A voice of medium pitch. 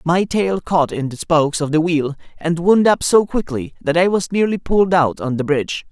Yes: medium, 165 Hz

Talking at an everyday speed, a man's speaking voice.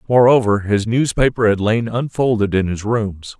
Yes: average, 160 wpm; male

